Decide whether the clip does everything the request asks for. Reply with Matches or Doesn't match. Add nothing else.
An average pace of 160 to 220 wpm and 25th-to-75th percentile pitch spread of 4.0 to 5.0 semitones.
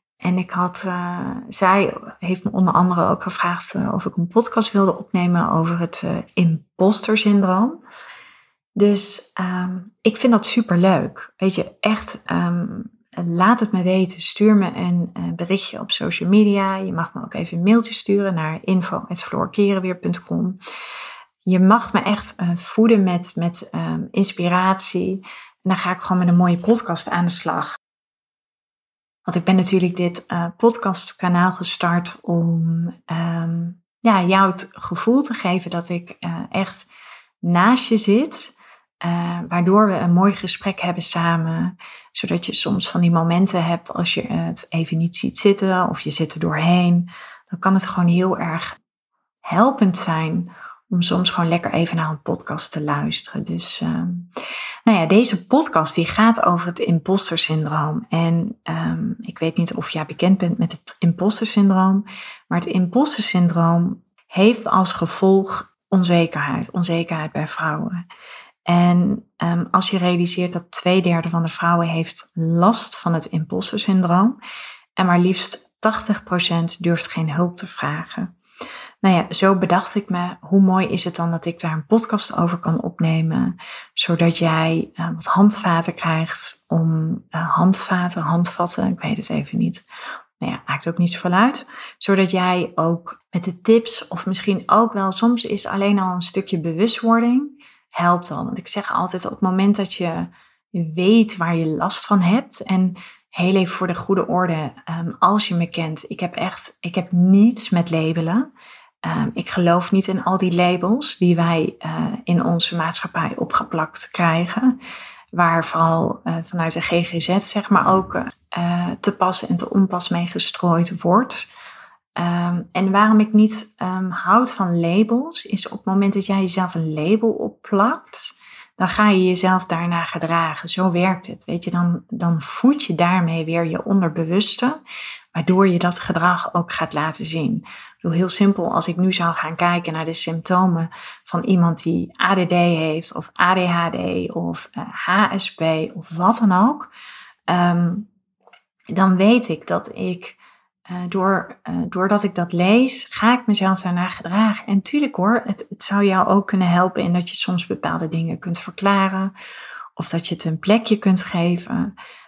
Doesn't match